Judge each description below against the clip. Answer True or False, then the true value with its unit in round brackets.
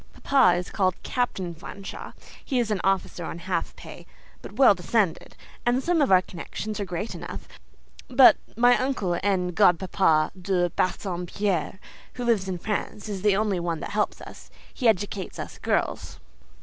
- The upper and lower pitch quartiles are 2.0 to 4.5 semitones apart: True (3.5 semitones)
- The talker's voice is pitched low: False (195 Hz)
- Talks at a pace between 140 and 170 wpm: True (160 wpm)